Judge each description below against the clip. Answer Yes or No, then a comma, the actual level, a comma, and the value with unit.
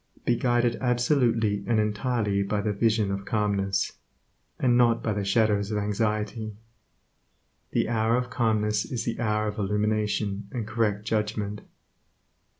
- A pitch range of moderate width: No, narrow, 1.9 semitones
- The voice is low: Yes, low, 105 Hz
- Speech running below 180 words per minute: Yes, average, 140 wpm